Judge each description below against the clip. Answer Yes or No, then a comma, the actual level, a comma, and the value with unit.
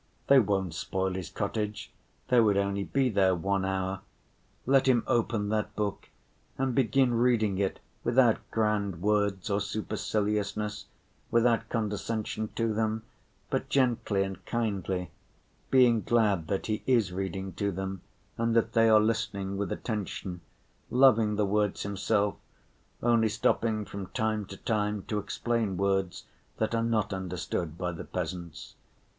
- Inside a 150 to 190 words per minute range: No, average, 140 wpm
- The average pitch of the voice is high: No, low, 105 Hz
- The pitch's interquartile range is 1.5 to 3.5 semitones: Yes, average, 2.8 semitones